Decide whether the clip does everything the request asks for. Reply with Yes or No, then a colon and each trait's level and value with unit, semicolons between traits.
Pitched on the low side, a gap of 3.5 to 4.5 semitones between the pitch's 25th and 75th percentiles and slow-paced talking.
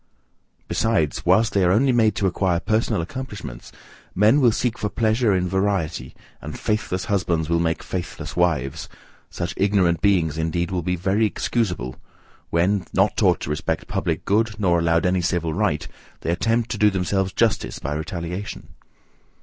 No: very low, 95 Hz; average, 4.0 semitones; average, 160 wpm